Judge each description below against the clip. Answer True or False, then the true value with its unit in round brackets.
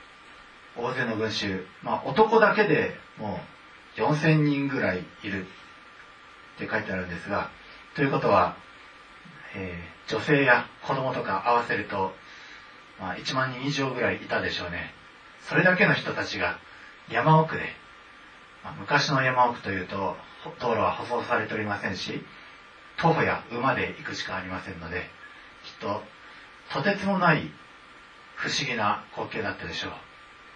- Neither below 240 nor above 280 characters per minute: True (275 characters per minute)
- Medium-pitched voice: False (130 Hz)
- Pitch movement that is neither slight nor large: False (6.7 semitones)